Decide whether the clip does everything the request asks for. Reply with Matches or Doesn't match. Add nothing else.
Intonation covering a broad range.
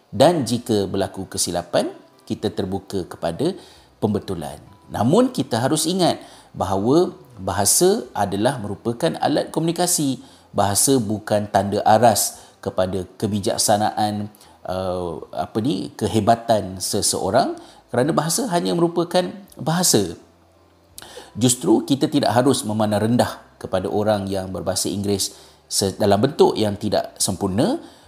Matches